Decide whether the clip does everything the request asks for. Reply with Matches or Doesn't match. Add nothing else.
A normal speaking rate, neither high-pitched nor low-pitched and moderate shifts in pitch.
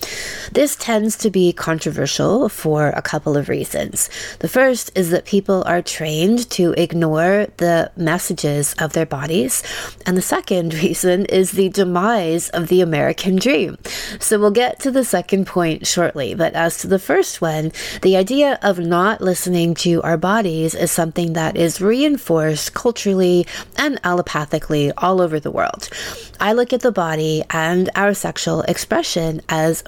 Matches